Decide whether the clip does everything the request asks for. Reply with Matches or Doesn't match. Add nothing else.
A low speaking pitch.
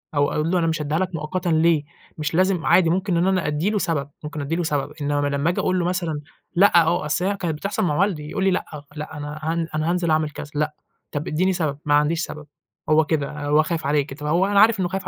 Doesn't match